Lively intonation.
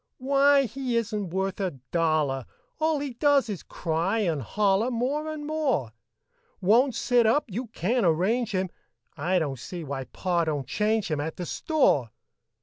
Yes: wide, 7.5 semitones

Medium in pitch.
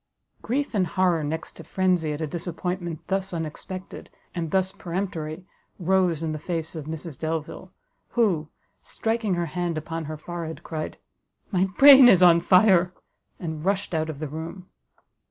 Yes: medium, 175 Hz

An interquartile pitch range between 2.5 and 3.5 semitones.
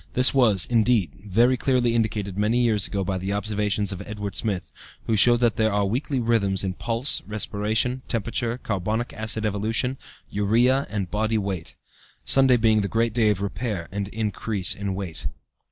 Yes: average, 2.8 semitones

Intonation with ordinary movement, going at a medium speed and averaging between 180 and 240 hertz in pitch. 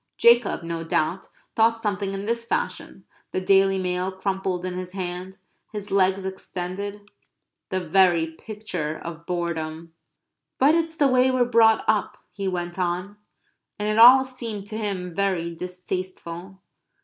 Yes: average, 3.1 semitones; average, 145 wpm; high, 190 Hz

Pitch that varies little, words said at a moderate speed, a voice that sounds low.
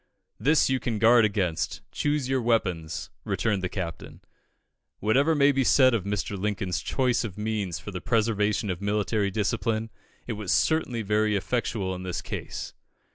No: average, 3.5 semitones; average, 160 wpm; low, 105 Hz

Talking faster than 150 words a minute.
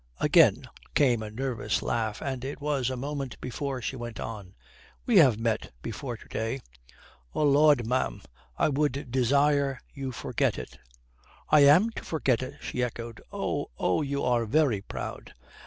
Yes: average, 160 wpm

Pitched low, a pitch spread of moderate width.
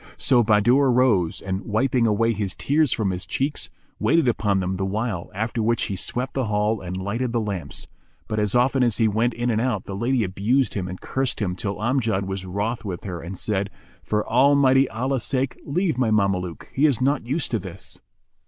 Yes: low, 110 Hz; average, 4.6 semitones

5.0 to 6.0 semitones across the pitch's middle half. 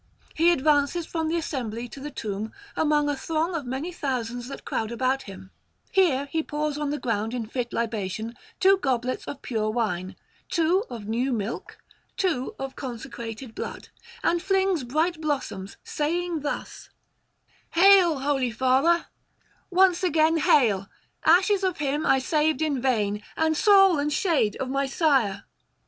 Yes: wide, 5.4 semitones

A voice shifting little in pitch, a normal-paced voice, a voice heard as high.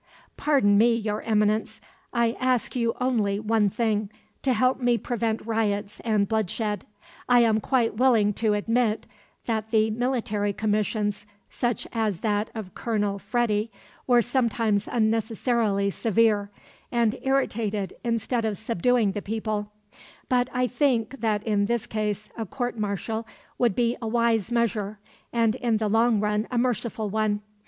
Yes: narrow, 2.2 semitones; average, 145 wpm; high, 220 Hz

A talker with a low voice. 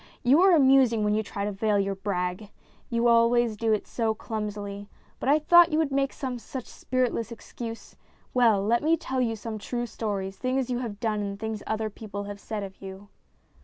No: high, 225 Hz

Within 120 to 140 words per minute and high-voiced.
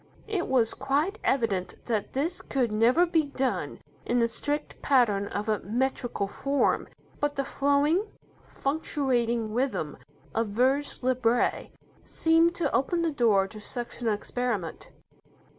Yes: slow, 135 wpm; very high, 255 Hz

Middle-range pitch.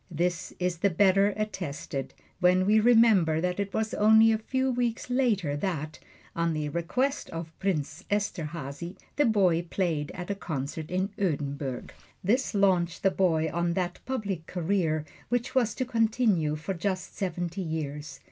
Yes: medium, 180 Hz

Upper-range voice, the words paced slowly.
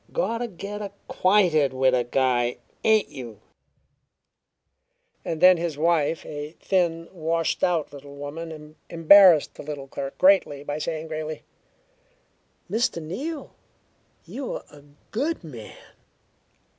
No: medium, 160 Hz; slow, 110 wpm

